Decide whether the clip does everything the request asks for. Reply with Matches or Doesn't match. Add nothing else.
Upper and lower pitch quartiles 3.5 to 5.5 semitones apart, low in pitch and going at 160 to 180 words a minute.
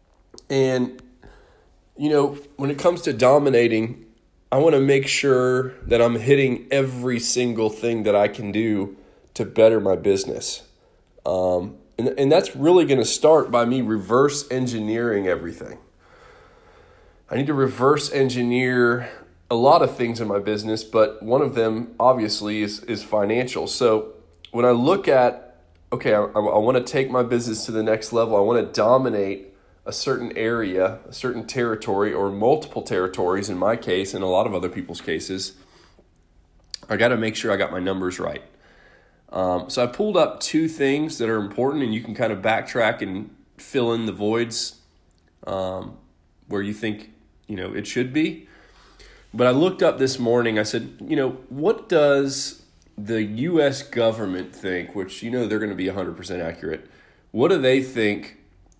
Matches